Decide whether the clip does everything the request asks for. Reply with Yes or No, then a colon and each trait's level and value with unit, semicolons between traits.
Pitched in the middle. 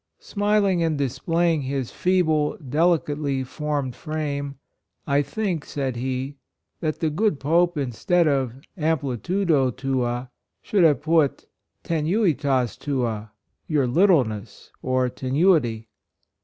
Yes: medium, 145 Hz